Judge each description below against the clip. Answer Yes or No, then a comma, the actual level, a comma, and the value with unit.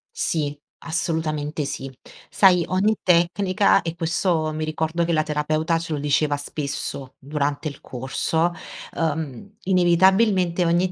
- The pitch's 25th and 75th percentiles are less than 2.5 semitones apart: No, average, 2.8 semitones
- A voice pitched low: No, medium, 160 Hz